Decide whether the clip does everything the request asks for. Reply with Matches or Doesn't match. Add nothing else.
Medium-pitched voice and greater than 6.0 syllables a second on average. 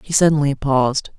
Doesn't match